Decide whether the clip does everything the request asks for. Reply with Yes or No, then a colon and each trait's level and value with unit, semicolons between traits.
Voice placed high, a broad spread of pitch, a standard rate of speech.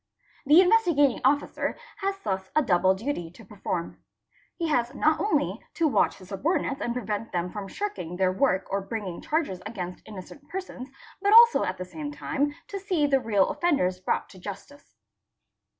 Yes: high, 245 Hz; wide, 8.6 semitones; average, 180 wpm